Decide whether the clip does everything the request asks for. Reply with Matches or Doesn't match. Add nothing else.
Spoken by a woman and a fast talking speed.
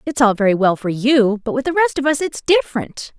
Matches